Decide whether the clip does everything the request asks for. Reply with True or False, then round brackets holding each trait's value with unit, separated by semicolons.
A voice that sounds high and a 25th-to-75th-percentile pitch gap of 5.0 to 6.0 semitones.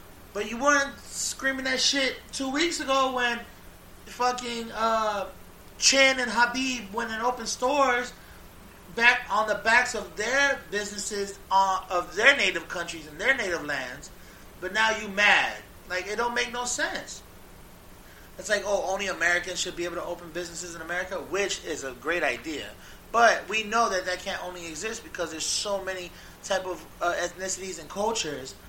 True (205 Hz; 5.3 semitones)